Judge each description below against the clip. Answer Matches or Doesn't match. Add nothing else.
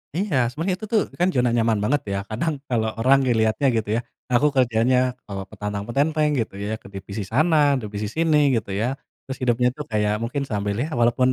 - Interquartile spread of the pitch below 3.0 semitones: Doesn't match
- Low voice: Matches